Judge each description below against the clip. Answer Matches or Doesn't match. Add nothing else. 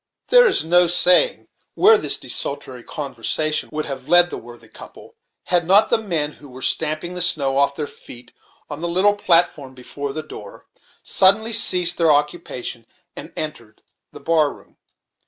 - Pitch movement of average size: Matches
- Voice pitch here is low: Doesn't match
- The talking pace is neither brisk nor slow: Matches